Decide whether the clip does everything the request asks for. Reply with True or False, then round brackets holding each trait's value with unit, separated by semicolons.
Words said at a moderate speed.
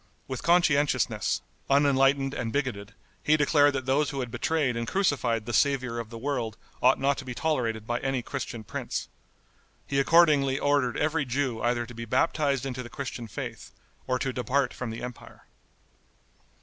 True (170 wpm)